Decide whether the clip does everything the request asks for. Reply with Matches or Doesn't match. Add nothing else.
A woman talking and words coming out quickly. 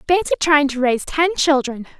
Doesn't match